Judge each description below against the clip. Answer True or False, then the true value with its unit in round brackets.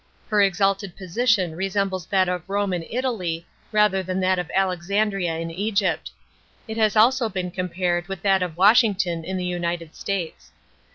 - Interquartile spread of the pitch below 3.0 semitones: True (2.5 semitones)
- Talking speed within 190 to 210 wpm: False (160 wpm)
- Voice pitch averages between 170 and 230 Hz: True (190 Hz)